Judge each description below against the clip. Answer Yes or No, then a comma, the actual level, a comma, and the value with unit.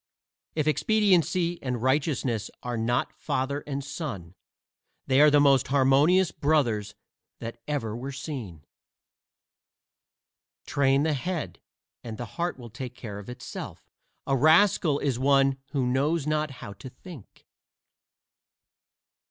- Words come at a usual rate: No, slow, 125 wpm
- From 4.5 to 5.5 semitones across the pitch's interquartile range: No, average, 3.8 semitones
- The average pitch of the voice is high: No, low, 135 Hz